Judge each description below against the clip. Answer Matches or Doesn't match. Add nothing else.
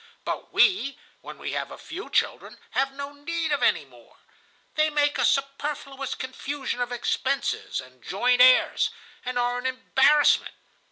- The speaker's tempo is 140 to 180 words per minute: Matches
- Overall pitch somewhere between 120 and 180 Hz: Doesn't match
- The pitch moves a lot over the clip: Doesn't match